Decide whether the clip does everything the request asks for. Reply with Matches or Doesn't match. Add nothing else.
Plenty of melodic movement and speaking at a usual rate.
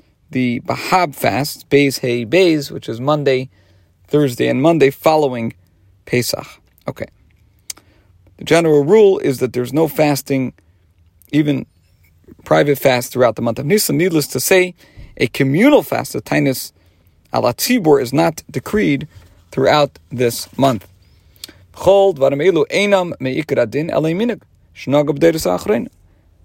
Doesn't match